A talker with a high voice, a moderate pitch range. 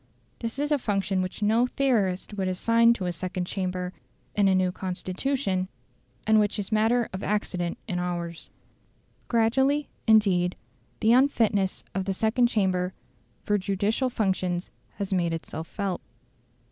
Yes: high, 195 Hz; average, 3.6 semitones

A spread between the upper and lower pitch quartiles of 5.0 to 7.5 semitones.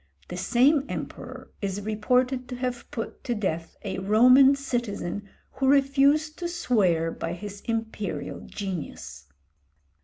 Yes: wide, 5.5 semitones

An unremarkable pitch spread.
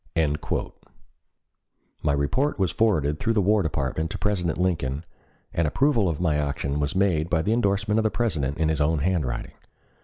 No: wide, 5.8 semitones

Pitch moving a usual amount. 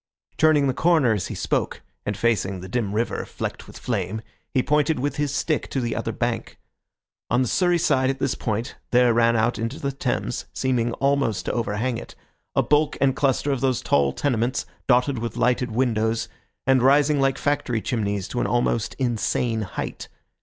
Yes: average, 3.4 semitones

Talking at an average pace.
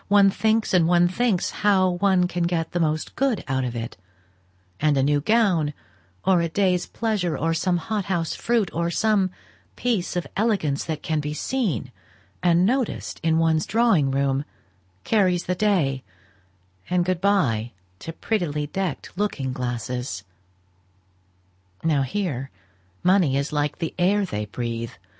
Yes: average, 150 wpm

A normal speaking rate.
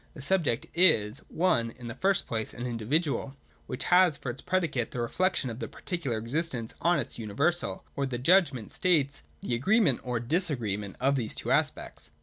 Yes: average, 175 wpm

